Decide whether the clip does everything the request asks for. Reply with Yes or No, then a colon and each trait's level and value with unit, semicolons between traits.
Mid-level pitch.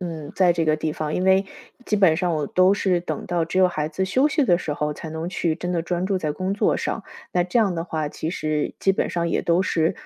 Yes: medium, 175 Hz